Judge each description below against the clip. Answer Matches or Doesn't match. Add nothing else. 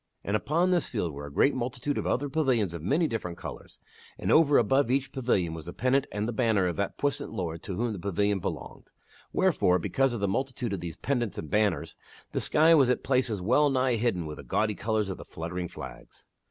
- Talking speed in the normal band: Doesn't match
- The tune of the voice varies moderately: Doesn't match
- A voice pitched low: Matches